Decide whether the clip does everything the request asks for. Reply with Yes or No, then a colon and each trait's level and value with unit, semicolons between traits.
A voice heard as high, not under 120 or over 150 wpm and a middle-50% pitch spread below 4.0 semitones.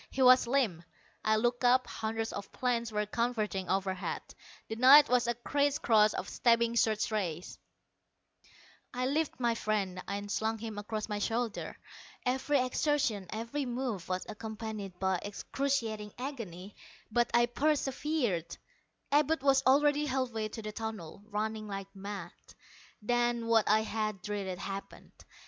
Yes: high, 225 Hz; average, 140 wpm; average, 3.4 semitones